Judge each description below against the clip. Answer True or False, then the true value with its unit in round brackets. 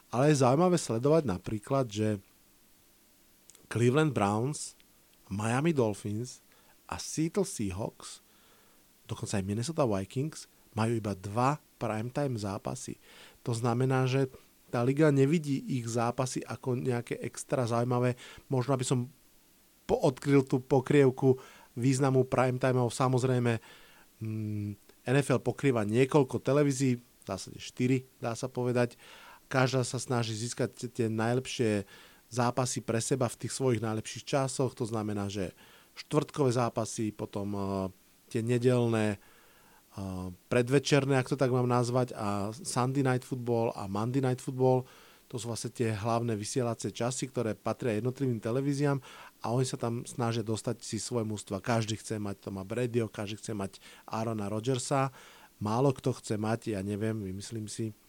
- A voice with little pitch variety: False (3.2 semitones)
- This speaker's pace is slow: False (135 wpm)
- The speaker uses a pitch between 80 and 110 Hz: False (120 Hz)